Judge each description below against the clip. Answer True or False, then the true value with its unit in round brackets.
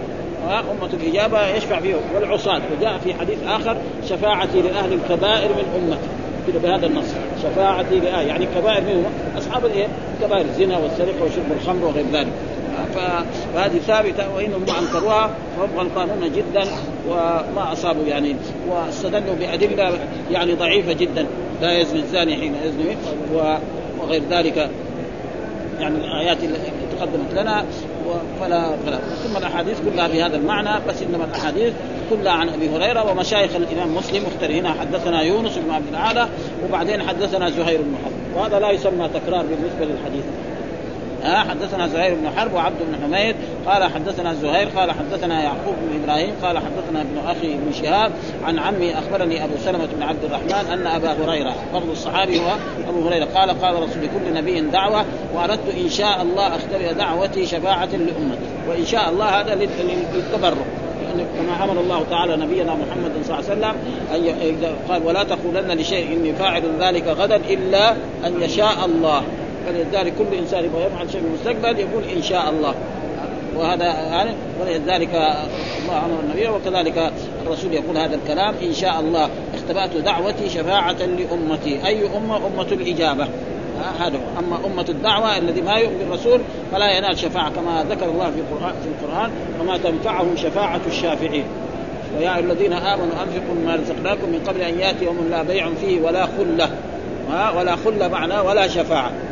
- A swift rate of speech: True (150 wpm)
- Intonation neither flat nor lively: True (3.0 semitones)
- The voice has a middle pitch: True (175 Hz)